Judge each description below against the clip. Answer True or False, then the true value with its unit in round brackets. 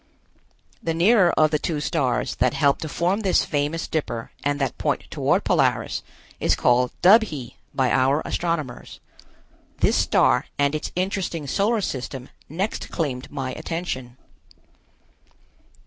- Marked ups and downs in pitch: False (4.6 semitones)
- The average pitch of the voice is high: False (150 Hz)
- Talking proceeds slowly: True (130 wpm)